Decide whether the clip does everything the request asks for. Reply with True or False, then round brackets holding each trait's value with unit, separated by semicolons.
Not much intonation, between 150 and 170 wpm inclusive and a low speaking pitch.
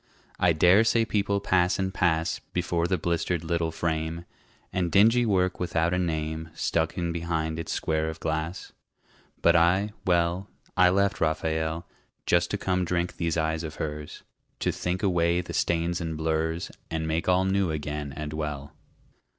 True (2.3 semitones; 165 wpm; 85 Hz)